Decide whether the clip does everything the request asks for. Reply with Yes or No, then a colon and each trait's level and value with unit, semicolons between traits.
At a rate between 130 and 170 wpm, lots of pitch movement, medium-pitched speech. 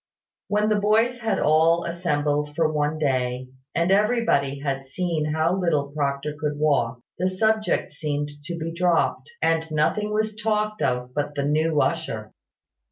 No: average, 160 wpm; average, 4.4 semitones; medium, 155 Hz